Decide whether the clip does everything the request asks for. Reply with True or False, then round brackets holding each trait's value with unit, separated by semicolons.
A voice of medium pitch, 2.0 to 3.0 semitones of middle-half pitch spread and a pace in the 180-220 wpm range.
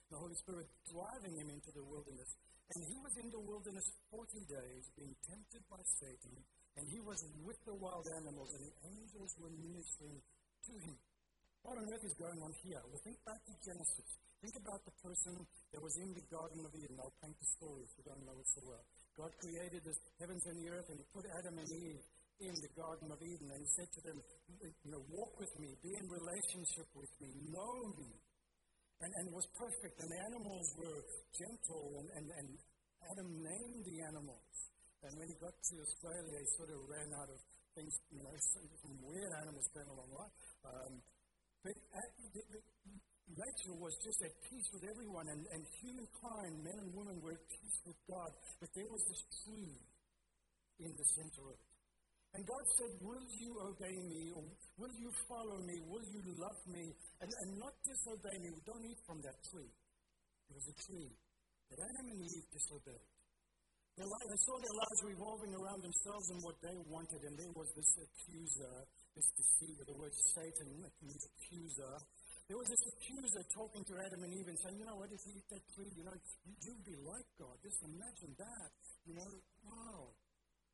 False (170 Hz; 4.6 semitones; 190 wpm)